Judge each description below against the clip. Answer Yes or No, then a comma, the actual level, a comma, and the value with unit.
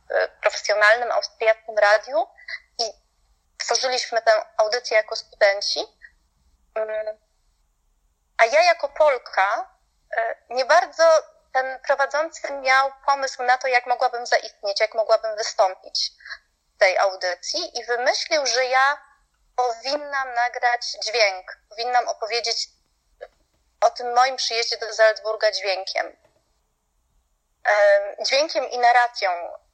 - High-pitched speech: Yes, high, 245 Hz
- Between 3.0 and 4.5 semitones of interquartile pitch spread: No, average, 5.3 semitones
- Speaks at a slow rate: Yes, slow, 100 wpm